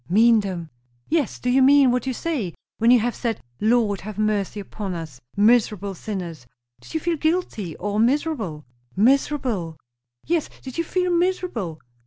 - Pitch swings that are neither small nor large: No, wide, 6.2 semitones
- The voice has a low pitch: No, high, 225 Hz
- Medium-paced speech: Yes, average, 160 wpm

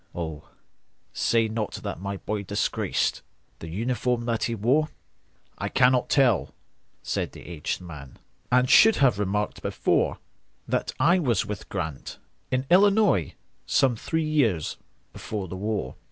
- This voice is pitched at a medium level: No, low, 110 Hz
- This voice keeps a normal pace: No, slow, 115 wpm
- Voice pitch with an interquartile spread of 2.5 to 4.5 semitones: No, wide, 5.4 semitones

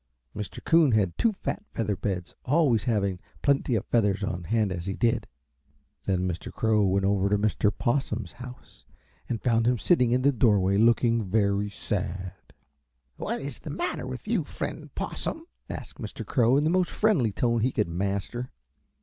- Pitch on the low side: Yes, low, 110 Hz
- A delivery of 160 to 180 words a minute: Yes, average, 175 wpm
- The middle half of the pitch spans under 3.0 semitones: No, average, 4.2 semitones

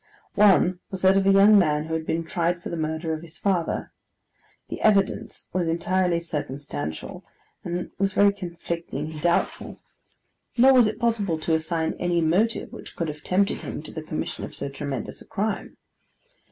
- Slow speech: No, average, 180 wpm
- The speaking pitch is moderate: Yes, medium, 170 Hz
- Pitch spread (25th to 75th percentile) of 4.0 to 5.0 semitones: No, average, 3.6 semitones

